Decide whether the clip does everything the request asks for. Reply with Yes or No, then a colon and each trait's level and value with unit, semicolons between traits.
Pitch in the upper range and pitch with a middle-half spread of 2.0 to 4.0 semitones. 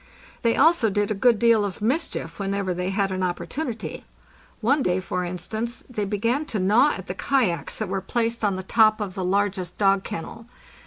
Yes: high, 205 Hz; average, 3.6 semitones